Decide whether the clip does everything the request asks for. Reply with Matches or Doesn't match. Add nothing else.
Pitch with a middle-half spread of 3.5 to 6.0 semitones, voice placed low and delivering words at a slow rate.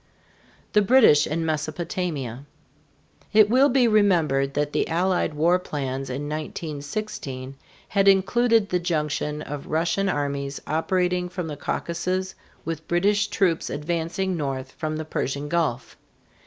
Doesn't match